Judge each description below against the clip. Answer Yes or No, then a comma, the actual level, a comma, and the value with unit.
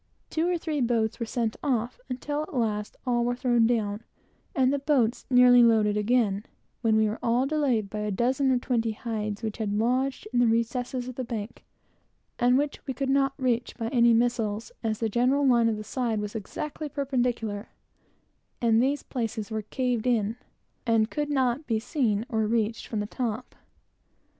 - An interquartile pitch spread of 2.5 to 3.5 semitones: Yes, average, 2.8 semitones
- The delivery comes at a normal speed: Yes, average, 185 wpm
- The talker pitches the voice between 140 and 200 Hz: No, high, 235 Hz